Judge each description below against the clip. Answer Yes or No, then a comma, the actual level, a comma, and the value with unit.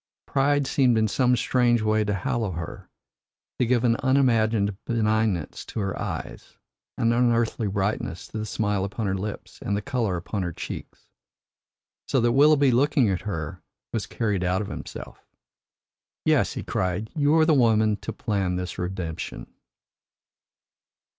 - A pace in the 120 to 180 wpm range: Yes, average, 155 wpm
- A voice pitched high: No, low, 110 Hz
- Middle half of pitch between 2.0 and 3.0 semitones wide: No, average, 4.0 semitones